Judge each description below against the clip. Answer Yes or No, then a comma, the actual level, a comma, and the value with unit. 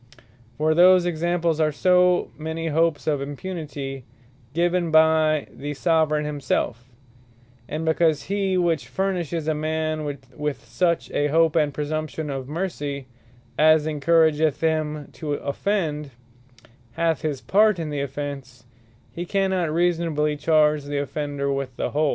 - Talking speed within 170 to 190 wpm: No, slow, 135 wpm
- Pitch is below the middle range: No, medium, 155 Hz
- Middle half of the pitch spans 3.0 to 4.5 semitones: No, narrow, 2.4 semitones